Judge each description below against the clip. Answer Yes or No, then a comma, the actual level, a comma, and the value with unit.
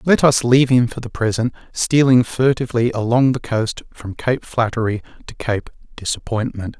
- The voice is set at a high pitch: No, low, 120 Hz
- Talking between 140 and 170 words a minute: Yes, average, 160 wpm